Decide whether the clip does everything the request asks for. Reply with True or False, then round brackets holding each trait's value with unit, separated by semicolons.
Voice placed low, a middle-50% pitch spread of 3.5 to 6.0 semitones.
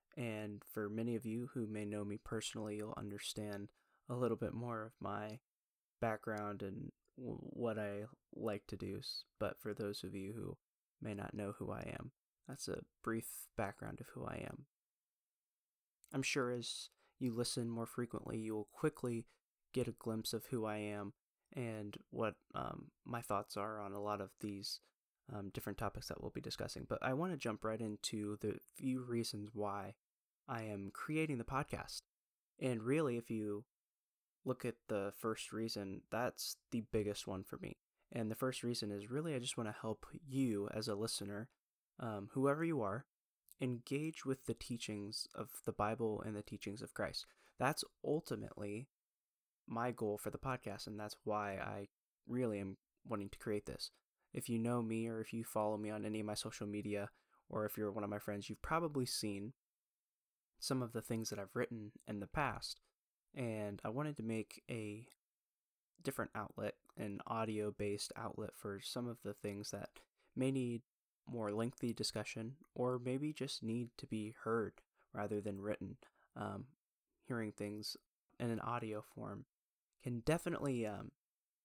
False (110 Hz; 2.8 semitones)